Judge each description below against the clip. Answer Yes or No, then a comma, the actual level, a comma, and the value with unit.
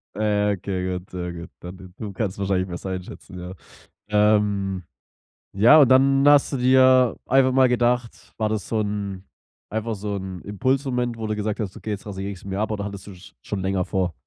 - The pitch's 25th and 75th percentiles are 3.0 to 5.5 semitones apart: Yes, average, 3.9 semitones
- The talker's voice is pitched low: Yes, low, 105 Hz